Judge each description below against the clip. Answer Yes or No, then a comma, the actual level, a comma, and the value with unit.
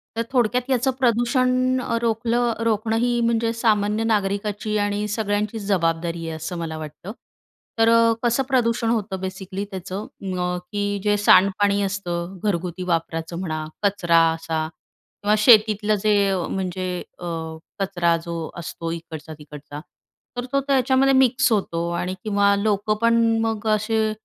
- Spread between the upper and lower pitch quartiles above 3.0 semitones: Yes, average, 4.3 semitones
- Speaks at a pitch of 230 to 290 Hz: No, high, 205 Hz